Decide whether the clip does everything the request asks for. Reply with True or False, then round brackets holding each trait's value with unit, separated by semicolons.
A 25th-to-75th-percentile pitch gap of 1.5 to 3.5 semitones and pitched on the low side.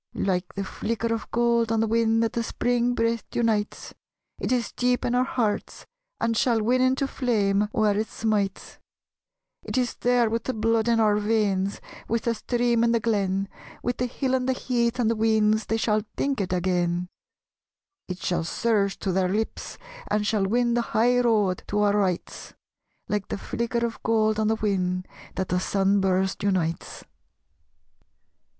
False (3.0 semitones; 220 Hz)